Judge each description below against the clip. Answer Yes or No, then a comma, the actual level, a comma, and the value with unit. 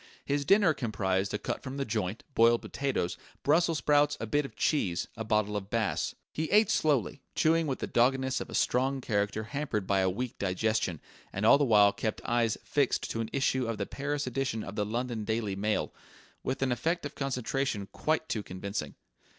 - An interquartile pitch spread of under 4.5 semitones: No, average, 4.9 semitones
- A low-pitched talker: Yes, low, 115 Hz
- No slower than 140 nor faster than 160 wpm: No, average, 195 wpm